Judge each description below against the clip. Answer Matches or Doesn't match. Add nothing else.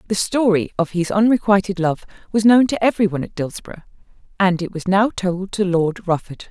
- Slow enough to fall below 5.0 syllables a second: Doesn't match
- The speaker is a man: Doesn't match